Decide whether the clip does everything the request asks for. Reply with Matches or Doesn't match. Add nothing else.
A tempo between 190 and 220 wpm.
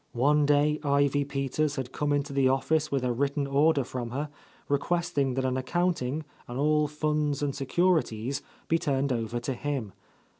Doesn't match